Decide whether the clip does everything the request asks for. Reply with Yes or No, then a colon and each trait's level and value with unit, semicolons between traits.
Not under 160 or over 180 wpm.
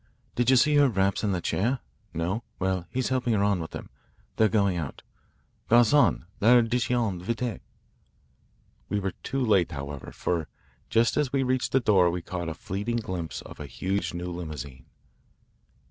Yes: average, 165 wpm